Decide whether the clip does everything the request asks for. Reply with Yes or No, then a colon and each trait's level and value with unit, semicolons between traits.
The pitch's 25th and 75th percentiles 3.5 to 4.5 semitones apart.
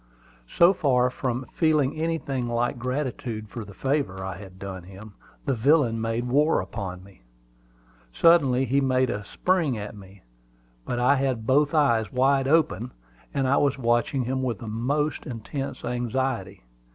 Yes: average, 4.1 semitones